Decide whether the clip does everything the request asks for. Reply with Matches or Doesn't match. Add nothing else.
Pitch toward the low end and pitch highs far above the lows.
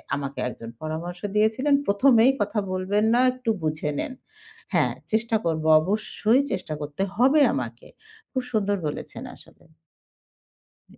Doesn't match